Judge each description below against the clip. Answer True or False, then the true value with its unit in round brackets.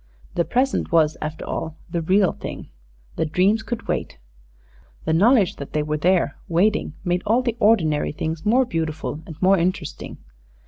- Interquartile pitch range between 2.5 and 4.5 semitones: False (5.1 semitones)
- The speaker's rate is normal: True (165 wpm)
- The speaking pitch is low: False (175 Hz)